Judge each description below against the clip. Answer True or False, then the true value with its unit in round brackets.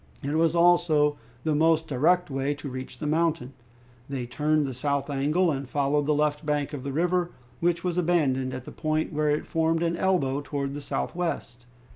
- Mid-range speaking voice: True (150 Hz)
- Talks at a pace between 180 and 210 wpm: True (190 wpm)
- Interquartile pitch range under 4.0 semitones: True (3.1 semitones)